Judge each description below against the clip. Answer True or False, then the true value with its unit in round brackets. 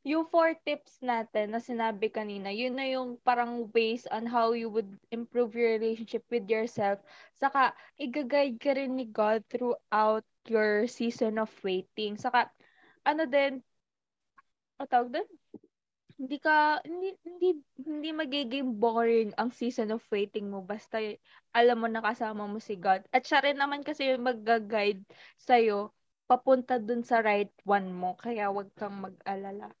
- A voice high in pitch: True (235 Hz)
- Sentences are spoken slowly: False (150 wpm)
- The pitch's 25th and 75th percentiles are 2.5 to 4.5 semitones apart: True (3.7 semitones)